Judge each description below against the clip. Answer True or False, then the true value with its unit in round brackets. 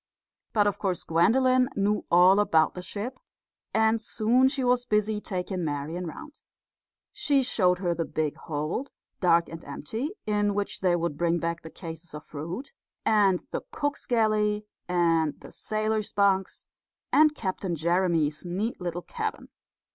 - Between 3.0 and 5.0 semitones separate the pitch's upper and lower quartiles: True (4.5 semitones)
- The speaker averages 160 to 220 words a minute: False (150 wpm)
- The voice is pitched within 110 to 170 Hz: False (195 Hz)